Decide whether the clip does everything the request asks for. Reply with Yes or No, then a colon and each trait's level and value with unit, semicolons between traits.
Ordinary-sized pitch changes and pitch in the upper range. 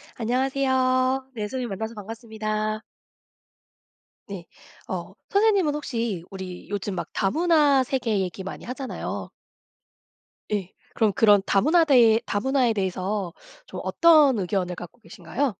Yes: average, 5.0 semitones; high, 225 Hz